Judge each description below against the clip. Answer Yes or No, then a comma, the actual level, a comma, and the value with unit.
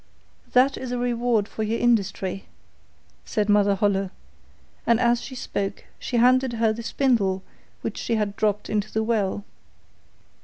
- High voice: Yes, high, 220 Hz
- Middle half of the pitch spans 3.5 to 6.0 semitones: No, average, 2.9 semitones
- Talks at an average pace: Yes, average, 150 wpm